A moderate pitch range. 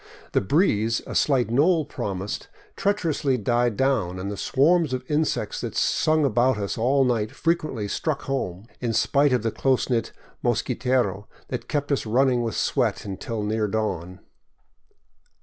Yes: average, 4.7 semitones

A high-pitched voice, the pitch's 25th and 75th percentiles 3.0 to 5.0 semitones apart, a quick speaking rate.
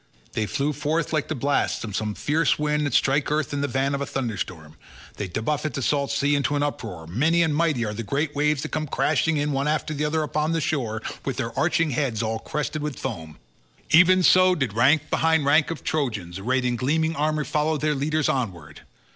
No: medium, 145 Hz; average, 4.5 semitones; fast, 210 wpm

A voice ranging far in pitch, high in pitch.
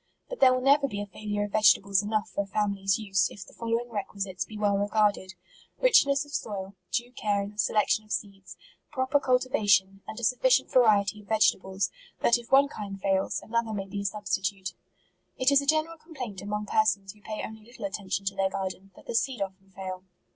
No: average, 3.4 semitones; high, 210 Hz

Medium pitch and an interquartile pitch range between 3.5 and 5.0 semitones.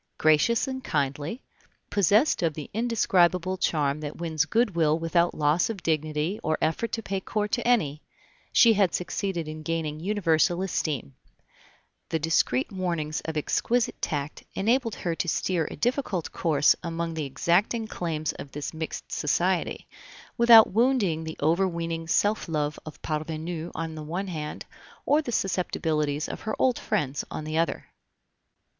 Yes: medium, 165 Hz; average, 4.4 semitones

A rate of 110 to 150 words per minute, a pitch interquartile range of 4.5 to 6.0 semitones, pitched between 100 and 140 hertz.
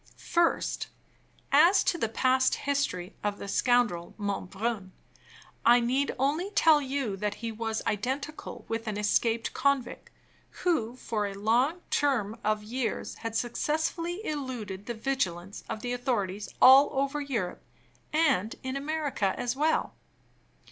No: slow, 135 wpm; average, 5.0 semitones; high, 245 Hz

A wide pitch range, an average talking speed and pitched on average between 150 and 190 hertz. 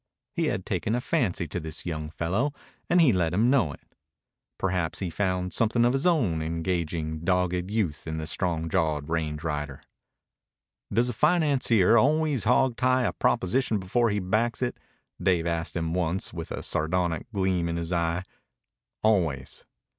No: wide, 6.0 semitones; average, 160 wpm; very low, 90 Hz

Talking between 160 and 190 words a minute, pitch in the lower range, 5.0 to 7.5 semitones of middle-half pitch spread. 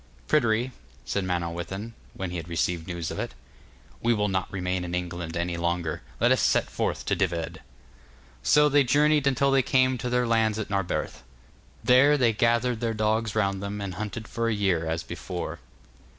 Yes: average, 180 wpm; low, 105 Hz; average, 5.3 semitones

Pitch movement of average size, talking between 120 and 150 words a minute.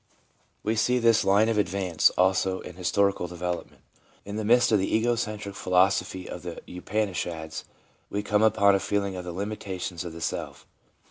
No: average, 3.0 semitones; average, 185 wpm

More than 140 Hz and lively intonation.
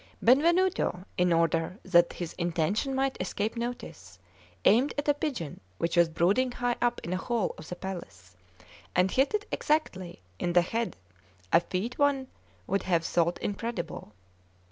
Yes: high, 190 Hz; wide, 6.4 semitones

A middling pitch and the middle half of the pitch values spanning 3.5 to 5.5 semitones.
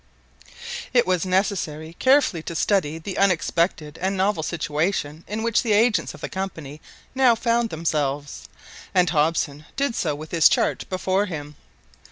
Yes: medium, 175 Hz; average, 4.8 semitones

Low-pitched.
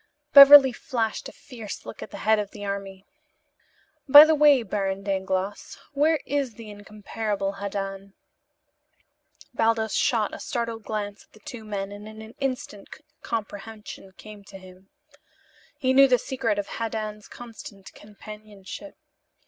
No: high, 215 Hz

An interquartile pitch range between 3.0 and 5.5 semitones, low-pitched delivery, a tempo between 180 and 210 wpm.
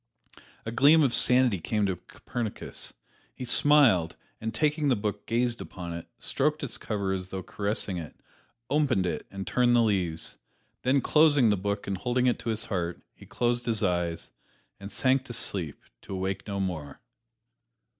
No: average, 4.8 semitones; low, 110 Hz; average, 170 wpm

